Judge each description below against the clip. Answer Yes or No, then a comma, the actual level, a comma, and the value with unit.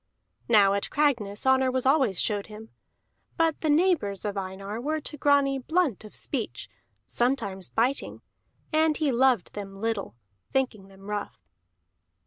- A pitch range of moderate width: No, wide, 5.9 semitones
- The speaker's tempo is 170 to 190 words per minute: No, average, 140 wpm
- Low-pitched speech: No, high, 240 Hz